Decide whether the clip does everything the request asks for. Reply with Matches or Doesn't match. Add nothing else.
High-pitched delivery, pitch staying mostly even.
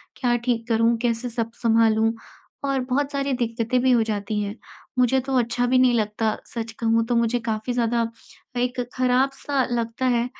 Matches